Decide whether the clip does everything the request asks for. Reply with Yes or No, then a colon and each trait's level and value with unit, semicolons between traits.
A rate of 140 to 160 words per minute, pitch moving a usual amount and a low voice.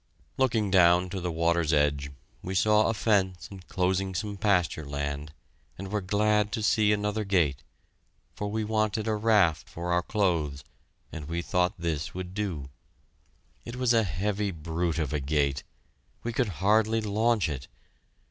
Yes: average, 155 wpm; average, 4.6 semitones; very low, 95 Hz